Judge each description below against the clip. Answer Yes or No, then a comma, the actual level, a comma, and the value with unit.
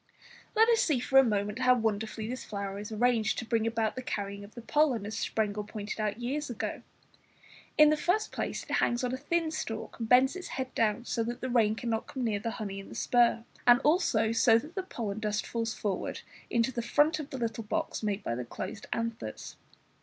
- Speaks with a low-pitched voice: No, high, 230 Hz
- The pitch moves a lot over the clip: No, average, 3.3 semitones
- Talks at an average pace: No, fast, 220 wpm